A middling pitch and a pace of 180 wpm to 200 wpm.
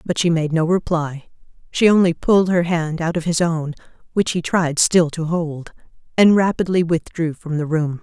Yes: medium, 165 Hz; average, 195 wpm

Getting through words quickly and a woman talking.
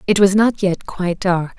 Yes: fast, 225 wpm; female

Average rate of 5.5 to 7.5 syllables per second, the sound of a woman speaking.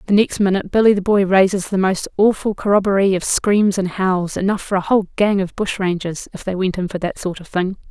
Yes: 5.8 syllables/s; female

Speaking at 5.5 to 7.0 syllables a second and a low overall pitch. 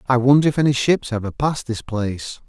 Yes: 5.8 syllables/s; low, 125 Hz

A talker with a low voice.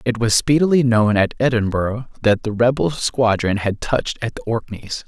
Yes: low, 115 Hz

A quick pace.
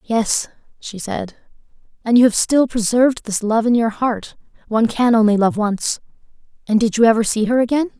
No: average, 175 wpm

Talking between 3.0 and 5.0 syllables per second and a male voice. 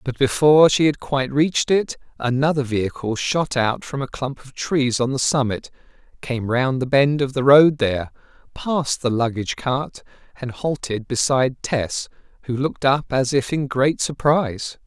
Yes: 4.9 syllables/s; male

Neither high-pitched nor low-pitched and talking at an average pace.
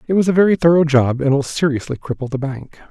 No: medium, 145 Hz; fast, 250 wpm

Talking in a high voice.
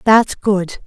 Yes: high, 205 Hz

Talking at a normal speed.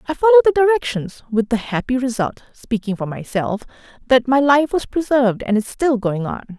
Yes: average, 175 wpm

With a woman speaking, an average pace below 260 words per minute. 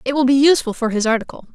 No: female; fast, 275 wpm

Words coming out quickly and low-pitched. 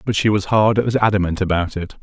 Yes: fast, 235 wpm; low, 100 Hz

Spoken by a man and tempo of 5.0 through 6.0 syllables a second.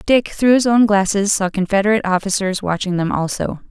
No: female; 5.7 syllables/s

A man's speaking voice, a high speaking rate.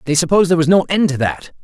Yes: male; fast, 295 wpm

